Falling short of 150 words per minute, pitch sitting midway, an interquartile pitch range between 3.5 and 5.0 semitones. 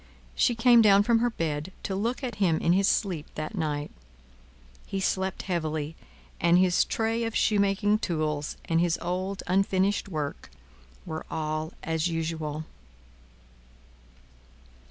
Yes: slow, 135 wpm; medium, 180 Hz; average, 4.2 semitones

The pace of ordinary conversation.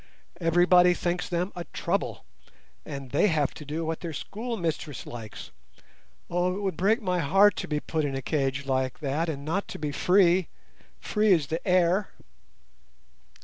Yes: average, 160 wpm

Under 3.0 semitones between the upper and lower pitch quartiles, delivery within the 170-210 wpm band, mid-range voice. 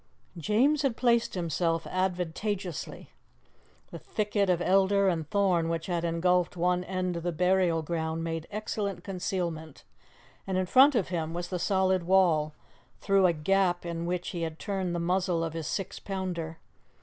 No: narrow, 2.5 semitones; average, 160 wpm; medium, 180 Hz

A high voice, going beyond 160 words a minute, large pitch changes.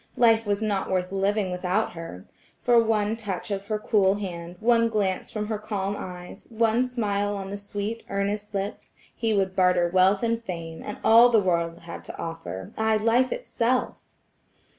No: high, 205 Hz; average, 170 wpm; average, 3.0 semitones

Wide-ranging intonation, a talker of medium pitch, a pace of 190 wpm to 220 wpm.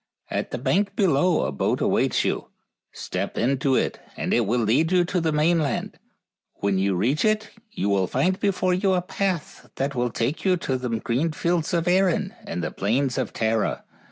Yes: wide, 7.4 semitones; medium, 150 Hz; average, 195 wpm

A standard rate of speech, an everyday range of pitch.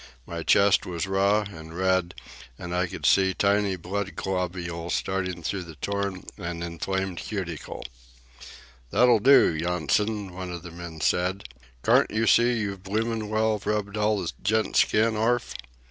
Yes: average, 150 wpm; average, 3.2 semitones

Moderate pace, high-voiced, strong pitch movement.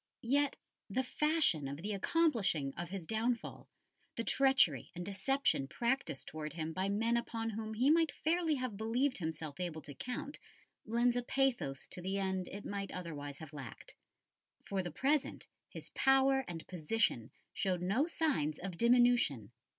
Yes: average, 160 wpm; high, 205 Hz; wide, 7.8 semitones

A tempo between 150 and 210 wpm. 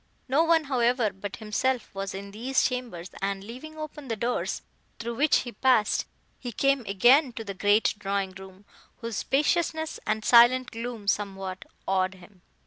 Yes: average, 160 wpm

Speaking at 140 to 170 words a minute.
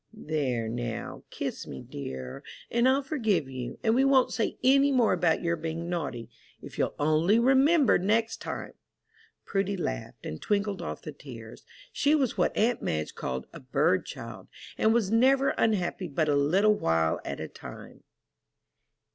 Yes: average, 165 wpm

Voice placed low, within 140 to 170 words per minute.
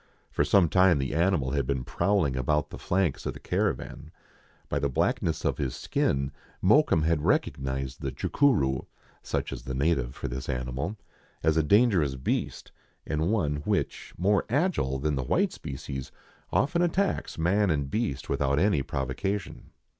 Yes: very low, 75 Hz; average, 160 wpm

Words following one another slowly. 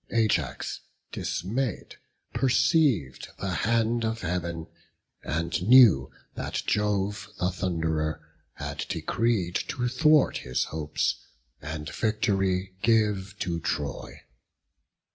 Yes: slow, 95 wpm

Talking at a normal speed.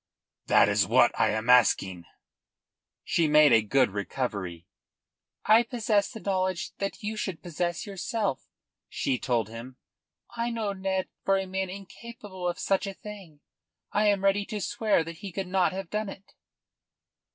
Yes: average, 160 wpm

